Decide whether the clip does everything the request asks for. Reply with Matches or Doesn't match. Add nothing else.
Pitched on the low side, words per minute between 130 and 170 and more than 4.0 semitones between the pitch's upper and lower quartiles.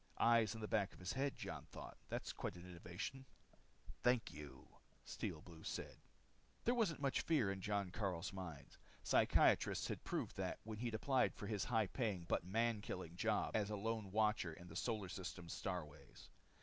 Doesn't match